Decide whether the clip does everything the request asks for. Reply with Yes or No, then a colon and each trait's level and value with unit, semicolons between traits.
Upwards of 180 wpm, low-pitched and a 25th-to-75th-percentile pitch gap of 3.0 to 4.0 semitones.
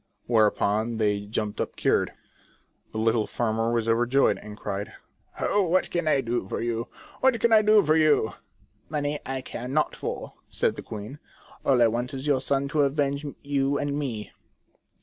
No: average, 190 wpm; low, 130 Hz; average, 4.5 semitones